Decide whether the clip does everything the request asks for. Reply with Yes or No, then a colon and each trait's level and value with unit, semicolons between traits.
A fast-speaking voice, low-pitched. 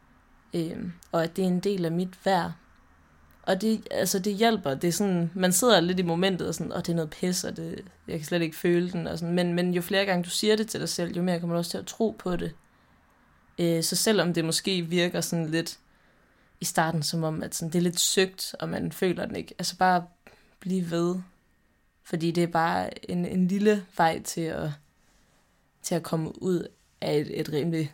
No: fast, 230 wpm; medium, 175 Hz